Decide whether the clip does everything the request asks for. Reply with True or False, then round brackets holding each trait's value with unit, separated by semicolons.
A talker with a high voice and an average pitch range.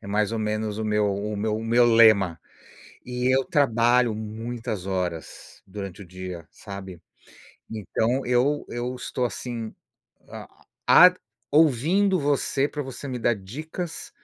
False (115 Hz; 3.8 semitones)